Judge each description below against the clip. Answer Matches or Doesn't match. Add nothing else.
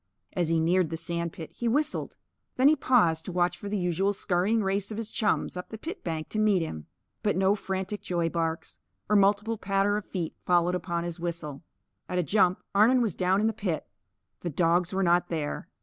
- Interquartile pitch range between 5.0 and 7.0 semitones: Doesn't match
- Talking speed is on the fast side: Matches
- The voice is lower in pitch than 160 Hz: Doesn't match